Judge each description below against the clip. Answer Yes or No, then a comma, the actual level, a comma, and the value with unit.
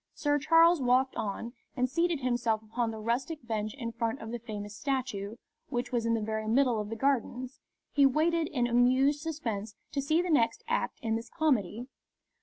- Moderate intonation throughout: Yes, average, 4.0 semitones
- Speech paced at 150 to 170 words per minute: No, average, 190 wpm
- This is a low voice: No, high, 245 Hz